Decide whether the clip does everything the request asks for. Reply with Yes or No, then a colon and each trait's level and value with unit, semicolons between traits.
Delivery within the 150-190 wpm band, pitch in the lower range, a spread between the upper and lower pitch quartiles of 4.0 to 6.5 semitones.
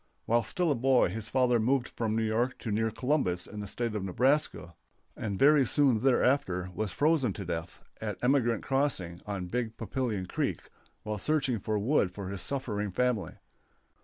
Yes: average, 175 wpm; low, 115 Hz; average, 4.5 semitones